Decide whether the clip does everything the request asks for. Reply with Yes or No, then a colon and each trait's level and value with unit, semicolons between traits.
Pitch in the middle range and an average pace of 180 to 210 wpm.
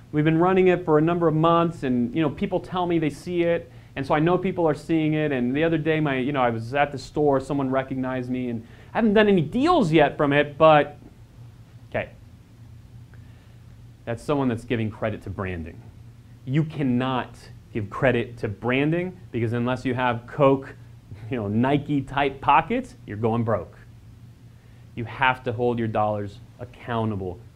No: low, 125 Hz; average, 185 wpm